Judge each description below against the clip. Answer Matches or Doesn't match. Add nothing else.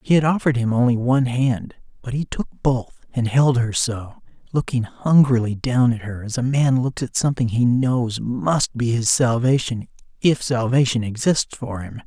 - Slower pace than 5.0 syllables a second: Matches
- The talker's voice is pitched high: Doesn't match